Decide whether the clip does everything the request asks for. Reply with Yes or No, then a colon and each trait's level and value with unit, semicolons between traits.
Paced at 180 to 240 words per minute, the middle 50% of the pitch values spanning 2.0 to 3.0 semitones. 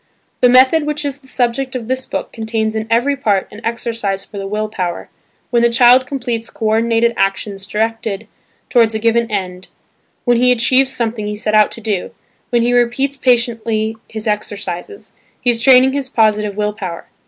Yes: average, 185 wpm; average, 2.7 semitones